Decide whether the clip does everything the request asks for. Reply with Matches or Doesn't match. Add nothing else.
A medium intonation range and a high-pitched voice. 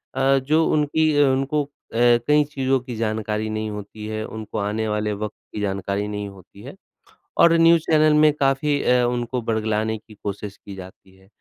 Doesn't match